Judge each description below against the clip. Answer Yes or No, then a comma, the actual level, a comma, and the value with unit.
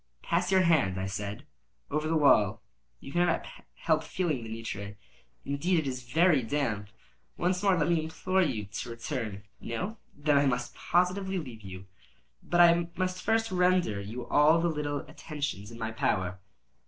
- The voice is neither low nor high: Yes, medium, 145 Hz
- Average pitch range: No, wide, 7.6 semitones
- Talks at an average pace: Yes, average, 165 wpm